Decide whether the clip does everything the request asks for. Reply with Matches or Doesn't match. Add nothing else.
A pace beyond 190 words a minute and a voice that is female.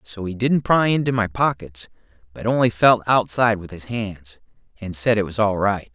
Doesn't match